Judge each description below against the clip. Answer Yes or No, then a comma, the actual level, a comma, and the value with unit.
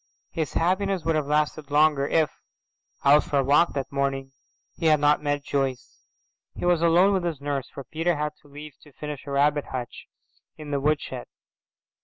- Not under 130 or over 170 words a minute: No, average, 180 wpm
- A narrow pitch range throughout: Yes, narrow, 2.1 semitones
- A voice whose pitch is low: No, medium, 150 Hz